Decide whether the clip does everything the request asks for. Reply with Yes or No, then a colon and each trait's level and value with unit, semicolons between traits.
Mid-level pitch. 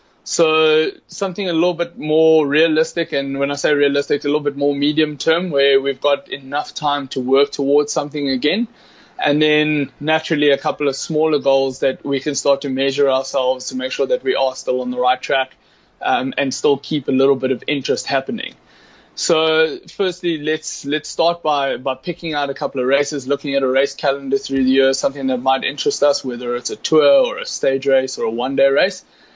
Yes: medium, 145 Hz